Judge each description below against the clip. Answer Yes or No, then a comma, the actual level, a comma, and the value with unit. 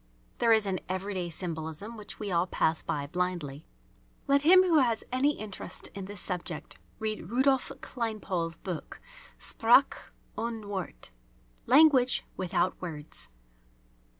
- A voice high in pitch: Yes, high, 200 Hz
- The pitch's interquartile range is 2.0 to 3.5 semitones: No, wide, 5.4 semitones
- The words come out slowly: Yes, slow, 125 wpm